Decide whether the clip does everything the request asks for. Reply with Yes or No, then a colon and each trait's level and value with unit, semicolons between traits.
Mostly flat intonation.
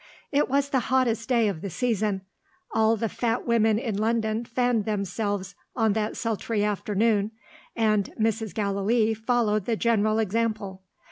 Yes: narrow, 1.9 semitones